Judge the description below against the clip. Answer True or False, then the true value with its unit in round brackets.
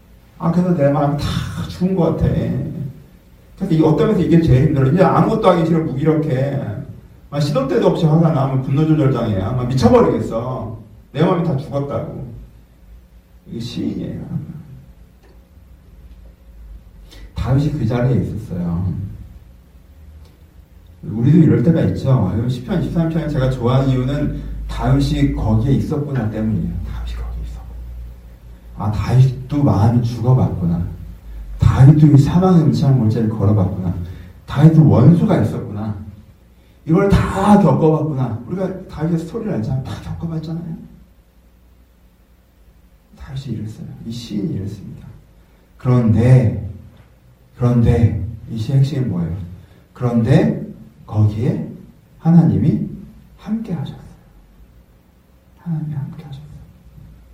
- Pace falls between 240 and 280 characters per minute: True (260 characters per minute)